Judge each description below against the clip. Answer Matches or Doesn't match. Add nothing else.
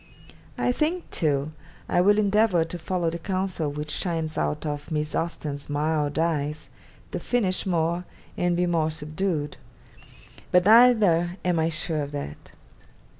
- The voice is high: Doesn't match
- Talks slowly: Doesn't match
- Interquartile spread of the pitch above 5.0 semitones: Doesn't match